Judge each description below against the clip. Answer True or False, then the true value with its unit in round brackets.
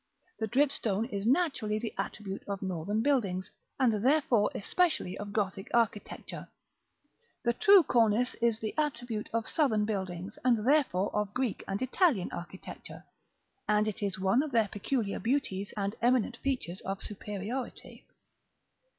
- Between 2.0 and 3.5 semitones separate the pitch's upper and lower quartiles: False (4.2 semitones)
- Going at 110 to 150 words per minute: True (140 wpm)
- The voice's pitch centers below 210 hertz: False (215 Hz)